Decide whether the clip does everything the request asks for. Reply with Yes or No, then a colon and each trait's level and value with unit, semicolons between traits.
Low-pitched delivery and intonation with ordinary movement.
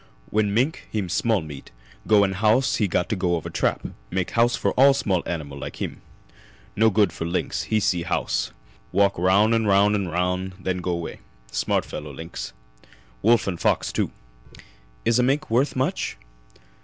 Yes: low, 100 Hz; average, 4.0 semitones